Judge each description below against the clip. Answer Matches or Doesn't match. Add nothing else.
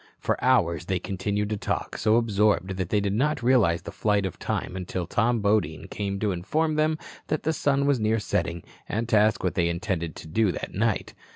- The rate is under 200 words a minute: Doesn't match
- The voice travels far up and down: Doesn't match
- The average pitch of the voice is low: Matches